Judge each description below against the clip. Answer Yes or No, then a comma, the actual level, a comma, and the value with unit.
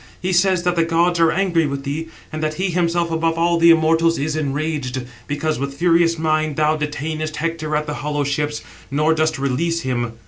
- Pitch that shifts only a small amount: Yes, narrow, 2.1 semitones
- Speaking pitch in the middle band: Yes, medium, 155 Hz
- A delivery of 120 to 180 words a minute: No, average, 200 wpm